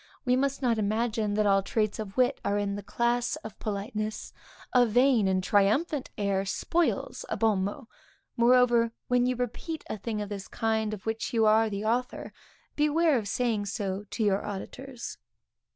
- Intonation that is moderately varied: Yes, average, 3.3 semitones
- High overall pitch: Yes, high, 220 Hz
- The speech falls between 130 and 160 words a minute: No, average, 175 wpm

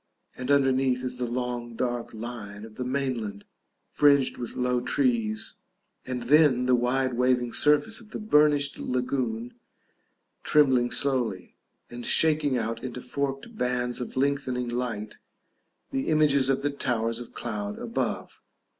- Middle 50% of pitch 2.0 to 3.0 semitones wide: Yes, narrow, 2.6 semitones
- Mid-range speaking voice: No, low, 125 Hz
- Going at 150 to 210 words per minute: No, slow, 135 wpm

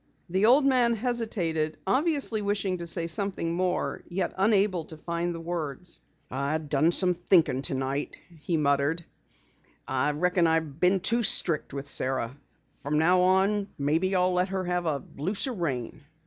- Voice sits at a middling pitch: Yes, medium, 175 Hz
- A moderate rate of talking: Yes, average, 155 wpm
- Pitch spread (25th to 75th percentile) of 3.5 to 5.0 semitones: Yes, average, 4.0 semitones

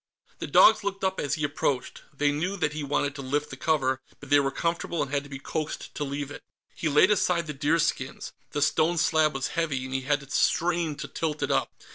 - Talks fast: Yes, fast, 235 wpm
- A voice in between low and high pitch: Yes, medium, 150 Hz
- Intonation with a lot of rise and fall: No, average, 2.8 semitones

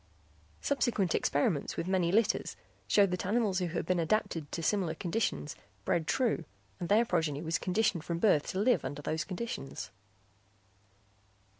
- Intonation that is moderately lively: Yes, average, 4.6 semitones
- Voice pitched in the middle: Yes, medium, 180 Hz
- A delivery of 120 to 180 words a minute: Yes, average, 150 wpm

